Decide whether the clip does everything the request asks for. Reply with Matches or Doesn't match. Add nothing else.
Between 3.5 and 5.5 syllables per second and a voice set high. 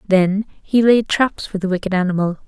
Matches